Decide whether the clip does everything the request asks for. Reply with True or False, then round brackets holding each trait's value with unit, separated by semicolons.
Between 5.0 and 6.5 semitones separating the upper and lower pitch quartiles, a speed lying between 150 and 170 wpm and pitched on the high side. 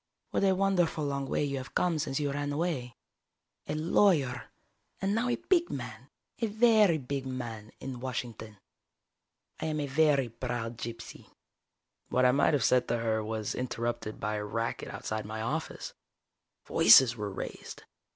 False (5.4 semitones; 160 wpm; 130 Hz)